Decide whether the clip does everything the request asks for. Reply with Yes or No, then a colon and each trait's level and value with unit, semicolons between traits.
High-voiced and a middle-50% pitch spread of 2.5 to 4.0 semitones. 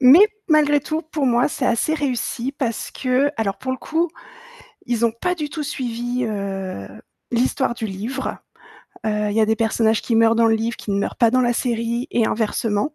Yes: high, 235 Hz; average, 3.5 semitones